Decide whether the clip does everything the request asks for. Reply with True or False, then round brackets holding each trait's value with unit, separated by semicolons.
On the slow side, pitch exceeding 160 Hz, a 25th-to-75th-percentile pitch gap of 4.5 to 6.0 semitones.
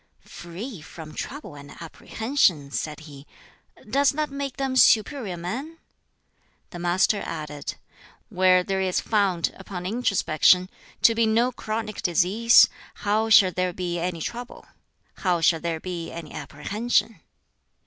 True (130 wpm; 185 Hz; 5.1 semitones)